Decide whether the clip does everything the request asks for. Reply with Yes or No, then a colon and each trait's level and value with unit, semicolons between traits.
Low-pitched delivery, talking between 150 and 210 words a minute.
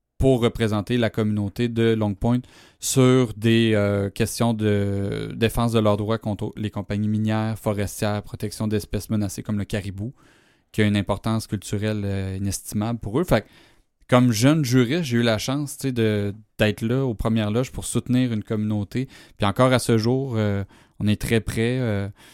Yes: low, 110 Hz; average, 175 wpm